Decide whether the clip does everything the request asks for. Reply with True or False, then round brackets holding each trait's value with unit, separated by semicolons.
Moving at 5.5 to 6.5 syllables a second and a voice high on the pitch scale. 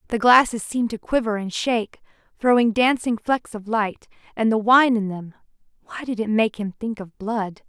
False (5.0 syllables/s; 225 Hz)